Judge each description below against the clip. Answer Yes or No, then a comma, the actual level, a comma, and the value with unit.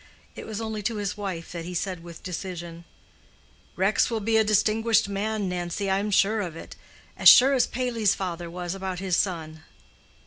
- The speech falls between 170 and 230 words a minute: Yes, average, 180 wpm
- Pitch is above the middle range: Yes, high, 195 Hz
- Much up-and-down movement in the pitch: No, average, 3.5 semitones